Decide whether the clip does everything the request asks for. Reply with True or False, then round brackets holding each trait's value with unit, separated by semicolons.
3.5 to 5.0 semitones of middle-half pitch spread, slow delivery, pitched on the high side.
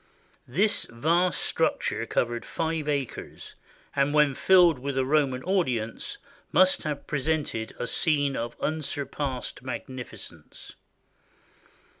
False (3.8 semitones; 110 wpm; 140 Hz)